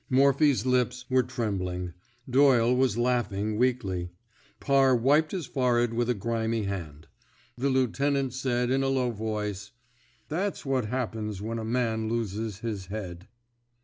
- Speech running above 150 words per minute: No, average, 145 wpm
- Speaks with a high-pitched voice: No, low, 120 Hz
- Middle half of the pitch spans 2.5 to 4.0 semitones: Yes, average, 3.5 semitones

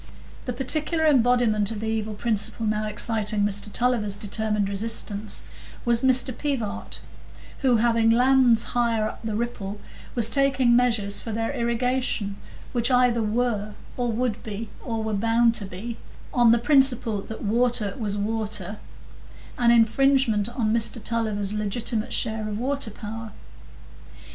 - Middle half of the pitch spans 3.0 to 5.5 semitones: No, narrow, 2.4 semitones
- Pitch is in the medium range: No, high, 225 Hz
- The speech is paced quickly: No, average, 140 wpm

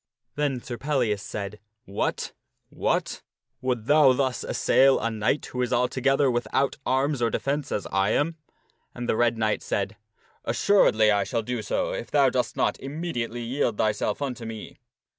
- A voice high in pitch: No, low, 125 Hz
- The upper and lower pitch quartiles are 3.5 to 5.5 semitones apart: Yes, average, 3.8 semitones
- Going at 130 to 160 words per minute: No, average, 170 wpm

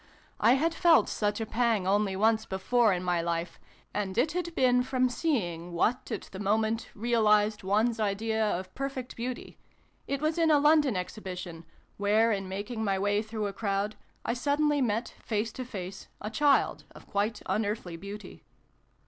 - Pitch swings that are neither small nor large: Yes, average, 4.0 semitones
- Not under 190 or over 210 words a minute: No, average, 170 wpm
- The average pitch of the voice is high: Yes, high, 215 Hz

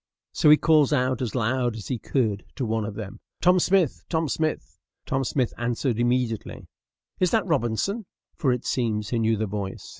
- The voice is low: Yes, low, 125 Hz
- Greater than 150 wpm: Yes, average, 185 wpm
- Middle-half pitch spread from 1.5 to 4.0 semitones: No, average, 5.2 semitones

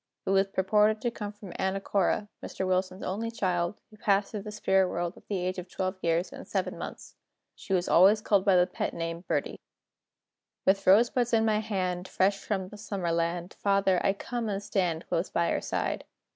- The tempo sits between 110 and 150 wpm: No, average, 200 wpm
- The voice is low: No, high, 195 Hz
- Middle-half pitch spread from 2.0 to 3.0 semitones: Yes, narrow, 2.4 semitones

